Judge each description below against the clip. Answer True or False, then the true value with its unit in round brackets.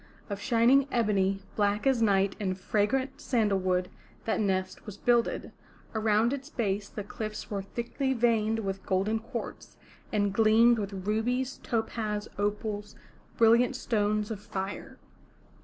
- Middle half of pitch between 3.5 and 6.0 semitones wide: False (2.6 semitones)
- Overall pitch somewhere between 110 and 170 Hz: False (215 Hz)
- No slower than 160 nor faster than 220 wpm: False (135 wpm)